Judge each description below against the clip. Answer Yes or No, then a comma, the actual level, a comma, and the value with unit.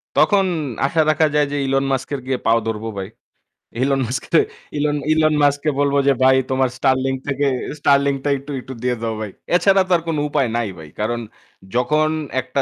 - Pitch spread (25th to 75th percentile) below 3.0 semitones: Yes, narrow, 2.6 semitones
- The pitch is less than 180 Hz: Yes, low, 135 Hz